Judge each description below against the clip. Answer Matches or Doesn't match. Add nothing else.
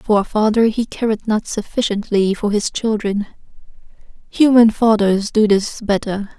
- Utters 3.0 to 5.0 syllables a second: Matches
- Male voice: Doesn't match